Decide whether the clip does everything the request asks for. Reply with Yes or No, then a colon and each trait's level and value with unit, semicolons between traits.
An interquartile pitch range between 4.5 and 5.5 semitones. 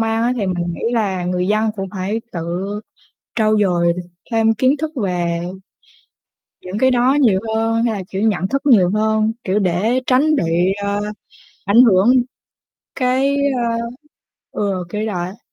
No: average, 4.1 semitones